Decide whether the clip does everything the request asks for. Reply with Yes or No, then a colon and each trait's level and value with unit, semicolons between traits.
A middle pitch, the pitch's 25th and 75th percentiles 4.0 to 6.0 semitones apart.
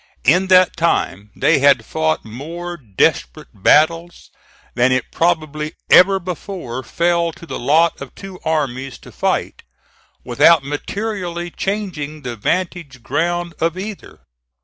Yes: medium, 165 Hz; average, 4.6 semitones